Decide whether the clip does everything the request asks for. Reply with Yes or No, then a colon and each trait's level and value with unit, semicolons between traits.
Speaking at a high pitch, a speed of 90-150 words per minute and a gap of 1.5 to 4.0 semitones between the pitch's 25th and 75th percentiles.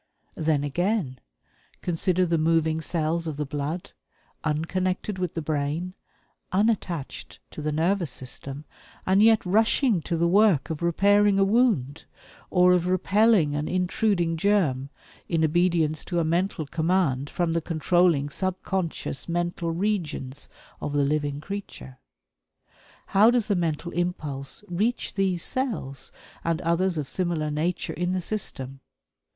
No: medium, 170 Hz; slow, 135 wpm; average, 3.7 semitones